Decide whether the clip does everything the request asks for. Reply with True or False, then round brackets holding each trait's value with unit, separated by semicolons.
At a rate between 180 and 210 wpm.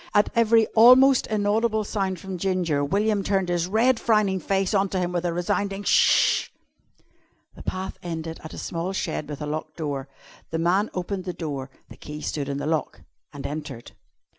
True (185 wpm)